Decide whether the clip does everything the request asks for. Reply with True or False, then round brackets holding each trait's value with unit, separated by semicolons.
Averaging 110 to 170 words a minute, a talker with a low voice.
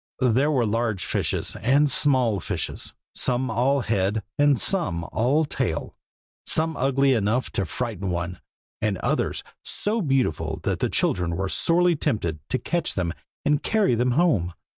True (150 wpm; 125 Hz)